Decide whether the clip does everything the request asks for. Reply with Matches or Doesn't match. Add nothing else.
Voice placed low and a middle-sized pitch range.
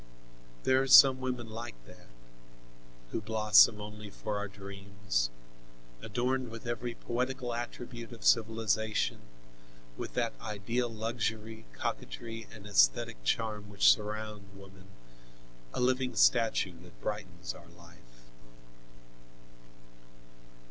Matches